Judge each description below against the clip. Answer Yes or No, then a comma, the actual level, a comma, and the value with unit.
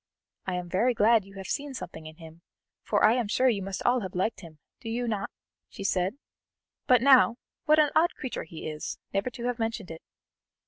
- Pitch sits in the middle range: No, high, 215 Hz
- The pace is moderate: No, fast, 215 wpm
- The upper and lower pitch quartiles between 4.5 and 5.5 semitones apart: Yes, average, 5.0 semitones